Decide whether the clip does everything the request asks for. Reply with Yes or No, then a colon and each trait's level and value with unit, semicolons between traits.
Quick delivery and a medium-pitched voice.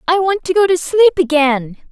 No: fast, 220 wpm; very high, 335 Hz